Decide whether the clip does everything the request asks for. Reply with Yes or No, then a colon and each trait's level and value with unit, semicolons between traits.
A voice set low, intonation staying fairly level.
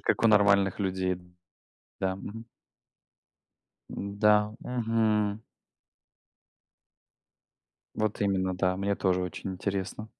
Yes: low, 100 Hz; narrow, 2.1 semitones